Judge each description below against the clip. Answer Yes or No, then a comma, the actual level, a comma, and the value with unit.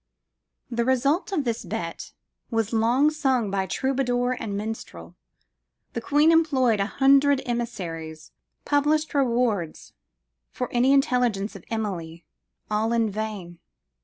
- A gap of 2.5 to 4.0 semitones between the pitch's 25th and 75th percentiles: No, average, 4.9 semitones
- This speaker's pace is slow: Yes, slow, 120 wpm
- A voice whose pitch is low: No, high, 235 Hz